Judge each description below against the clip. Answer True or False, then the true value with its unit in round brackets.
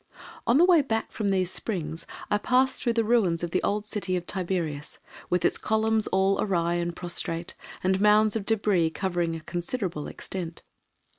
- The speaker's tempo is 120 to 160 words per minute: False (175 wpm)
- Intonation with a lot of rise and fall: False (4.1 semitones)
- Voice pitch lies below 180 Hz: False (190 Hz)